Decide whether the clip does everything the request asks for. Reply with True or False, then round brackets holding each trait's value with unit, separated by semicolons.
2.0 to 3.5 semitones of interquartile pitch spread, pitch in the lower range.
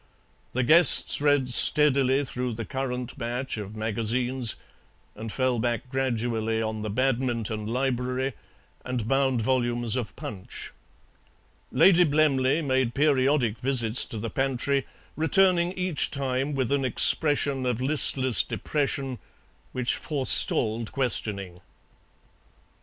True (2.9 semitones; 130 Hz)